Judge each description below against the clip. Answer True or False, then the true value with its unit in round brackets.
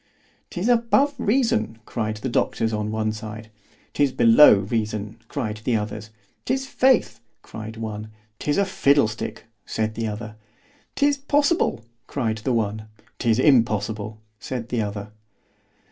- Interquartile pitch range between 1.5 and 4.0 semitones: False (4.9 semitones)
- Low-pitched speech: True (110 Hz)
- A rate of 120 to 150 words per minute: True (135 wpm)